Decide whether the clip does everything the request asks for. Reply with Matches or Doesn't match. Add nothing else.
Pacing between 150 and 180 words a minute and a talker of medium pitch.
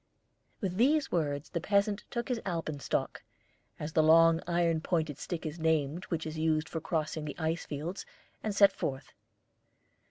Matches